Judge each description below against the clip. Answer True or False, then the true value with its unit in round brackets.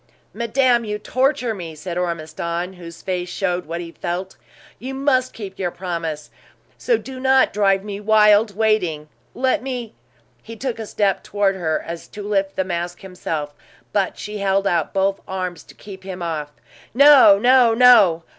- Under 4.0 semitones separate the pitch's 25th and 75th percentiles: False (4.5 semitones)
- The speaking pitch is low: False (195 Hz)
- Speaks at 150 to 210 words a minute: True (175 wpm)